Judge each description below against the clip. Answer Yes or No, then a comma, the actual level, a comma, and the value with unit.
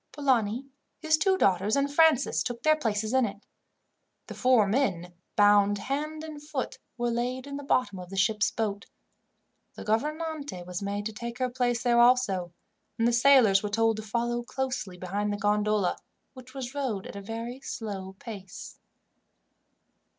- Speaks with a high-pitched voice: Yes, high, 235 Hz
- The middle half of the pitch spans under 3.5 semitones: No, average, 4.4 semitones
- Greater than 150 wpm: Yes, average, 165 wpm